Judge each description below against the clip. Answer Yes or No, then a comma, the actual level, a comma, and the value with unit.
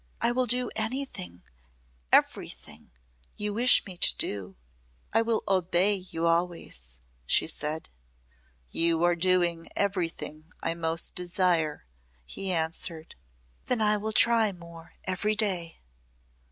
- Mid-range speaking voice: Yes, medium, 180 Hz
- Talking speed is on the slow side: Yes, slow, 120 wpm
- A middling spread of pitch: Yes, average, 4.2 semitones